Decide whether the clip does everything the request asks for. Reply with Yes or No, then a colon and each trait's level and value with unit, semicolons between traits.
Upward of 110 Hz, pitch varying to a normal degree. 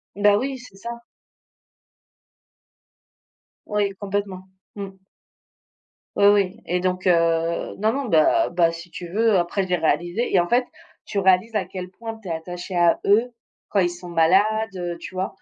Yes: high, 190 Hz; average, 3.2 semitones